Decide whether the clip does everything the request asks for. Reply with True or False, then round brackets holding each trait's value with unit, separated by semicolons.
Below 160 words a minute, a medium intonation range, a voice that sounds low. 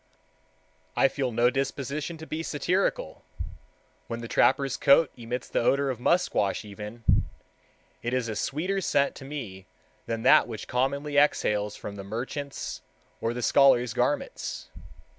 True (140 wpm; 3.8 semitones; 130 Hz)